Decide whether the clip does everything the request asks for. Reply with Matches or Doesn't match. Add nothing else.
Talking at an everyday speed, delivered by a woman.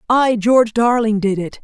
Matches